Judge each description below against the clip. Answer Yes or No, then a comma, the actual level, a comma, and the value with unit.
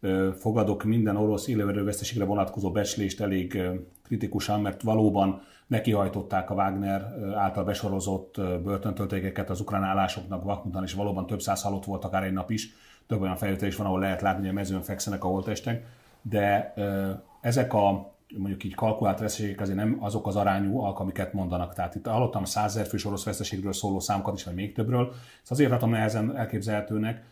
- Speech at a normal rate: No, fast, 175 wpm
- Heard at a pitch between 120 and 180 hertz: No, low, 100 Hz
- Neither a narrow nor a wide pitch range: No, narrow, 1.6 semitones